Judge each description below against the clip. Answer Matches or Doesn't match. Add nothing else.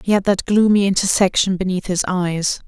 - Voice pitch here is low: Doesn't match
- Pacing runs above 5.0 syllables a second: Matches